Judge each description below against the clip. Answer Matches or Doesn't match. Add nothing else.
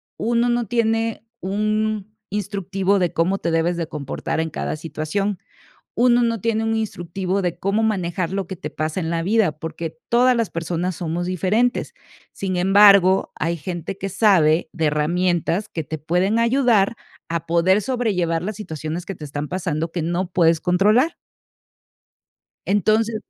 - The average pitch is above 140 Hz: Matches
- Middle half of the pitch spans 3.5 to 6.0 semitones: Matches